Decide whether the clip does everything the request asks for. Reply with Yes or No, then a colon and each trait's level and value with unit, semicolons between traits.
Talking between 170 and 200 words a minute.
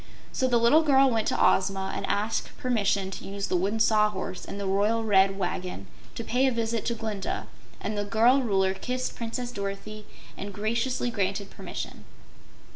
Yes: average, 175 wpm